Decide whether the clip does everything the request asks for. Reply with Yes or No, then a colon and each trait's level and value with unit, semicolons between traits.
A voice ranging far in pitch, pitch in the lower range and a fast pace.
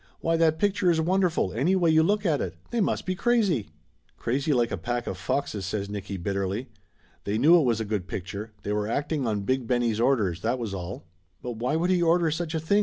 Yes: wide, 8.2 semitones; low, 125 Hz; fast, 235 wpm